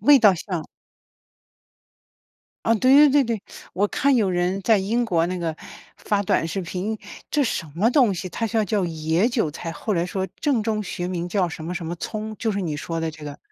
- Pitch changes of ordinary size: Yes, average, 4.6 semitones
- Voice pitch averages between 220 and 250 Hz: No, high, 195 Hz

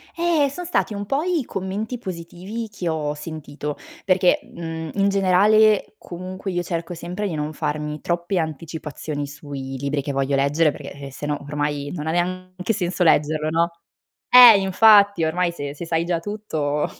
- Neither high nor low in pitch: Yes, medium, 170 Hz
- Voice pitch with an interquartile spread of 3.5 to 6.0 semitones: Yes, average, 4.8 semitones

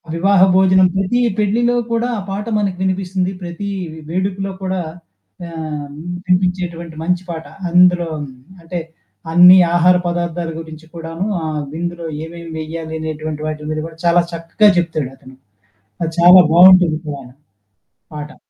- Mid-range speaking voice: Yes, medium, 175 Hz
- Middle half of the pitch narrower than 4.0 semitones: Yes, narrow, 2.5 semitones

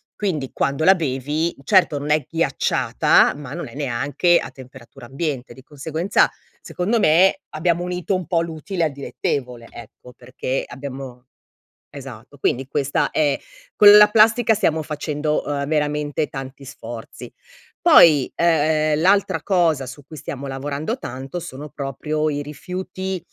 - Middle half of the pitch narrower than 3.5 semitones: No, average, 4.0 semitones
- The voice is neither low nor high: Yes, medium, 150 Hz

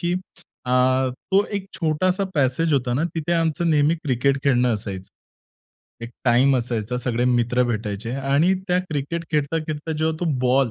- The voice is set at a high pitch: No, low, 135 Hz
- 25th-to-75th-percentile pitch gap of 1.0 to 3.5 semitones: No, average, 4.6 semitones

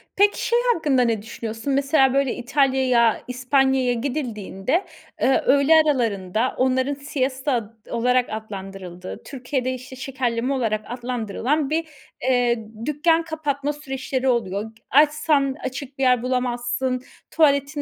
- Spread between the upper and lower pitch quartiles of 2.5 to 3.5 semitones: Yes, average, 3.0 semitones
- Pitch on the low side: No, very high, 255 Hz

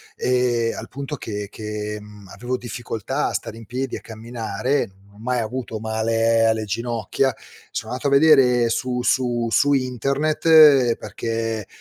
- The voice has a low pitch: Yes, low, 120 Hz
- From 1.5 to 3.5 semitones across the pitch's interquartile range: Yes, narrow, 2.6 semitones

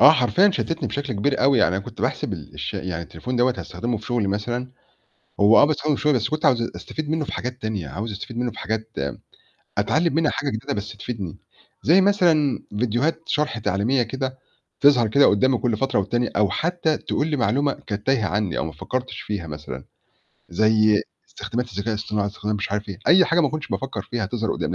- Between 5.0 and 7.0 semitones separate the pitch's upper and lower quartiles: Yes, average, 5.3 semitones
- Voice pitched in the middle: No, low, 120 Hz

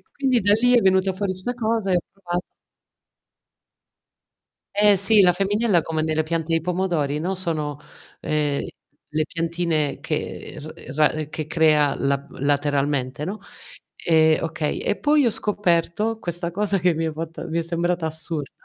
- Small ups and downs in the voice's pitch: No, average, 4.1 semitones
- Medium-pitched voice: Yes, medium, 170 Hz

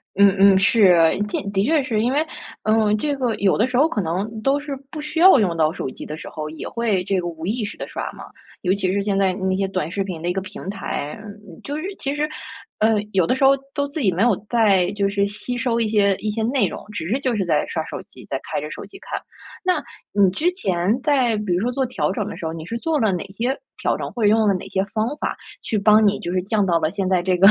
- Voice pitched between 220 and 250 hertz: No, high, 205 Hz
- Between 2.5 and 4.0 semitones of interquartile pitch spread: No, average, 4.4 semitones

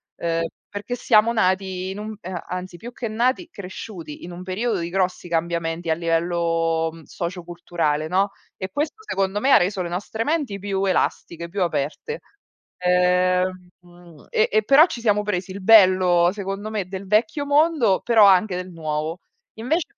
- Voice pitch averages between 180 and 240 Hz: Yes, medium, 185 Hz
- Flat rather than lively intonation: No, average, 3.7 semitones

